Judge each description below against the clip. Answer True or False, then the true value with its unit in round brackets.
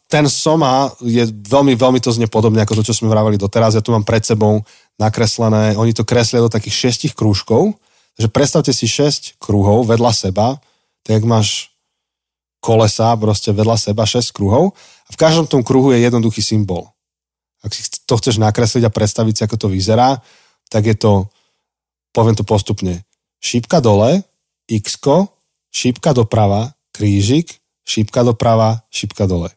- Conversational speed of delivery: True (155 wpm)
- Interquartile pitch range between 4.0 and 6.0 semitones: False (2.7 semitones)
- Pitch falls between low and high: False (115 Hz)